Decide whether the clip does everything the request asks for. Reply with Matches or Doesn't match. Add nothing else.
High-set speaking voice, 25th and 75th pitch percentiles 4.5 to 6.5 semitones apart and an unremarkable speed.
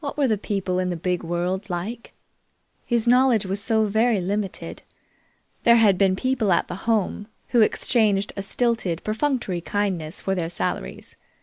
Doesn't match